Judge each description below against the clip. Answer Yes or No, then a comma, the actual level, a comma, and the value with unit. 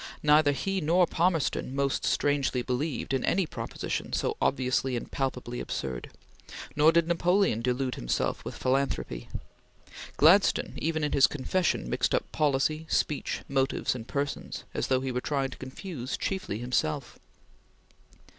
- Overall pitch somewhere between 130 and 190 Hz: Yes, medium, 140 Hz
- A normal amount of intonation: Yes, average, 3.9 semitones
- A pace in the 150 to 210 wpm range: No, average, 140 wpm